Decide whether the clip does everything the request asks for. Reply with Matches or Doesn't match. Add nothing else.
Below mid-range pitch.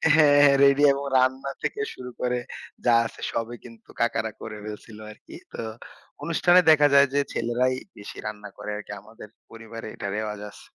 Matches